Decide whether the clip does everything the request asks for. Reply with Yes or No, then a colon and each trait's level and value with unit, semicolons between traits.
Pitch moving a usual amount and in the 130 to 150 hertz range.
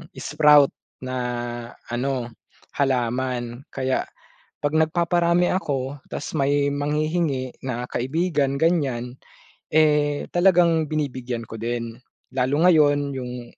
Yes: average, 3.6 semitones; medium, 140 Hz